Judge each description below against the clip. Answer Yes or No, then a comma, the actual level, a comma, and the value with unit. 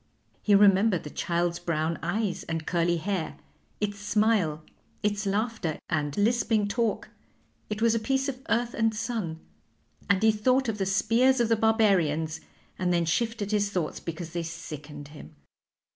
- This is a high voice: Yes, high, 200 Hz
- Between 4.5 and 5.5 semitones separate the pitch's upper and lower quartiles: Yes, average, 5.0 semitones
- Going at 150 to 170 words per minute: Yes, average, 160 wpm